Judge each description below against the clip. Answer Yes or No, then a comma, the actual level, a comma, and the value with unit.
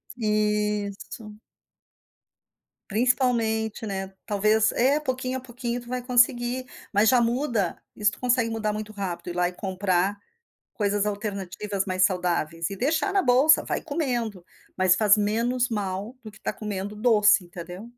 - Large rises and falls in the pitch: No, average, 3.6 semitones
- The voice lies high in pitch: Yes, high, 215 Hz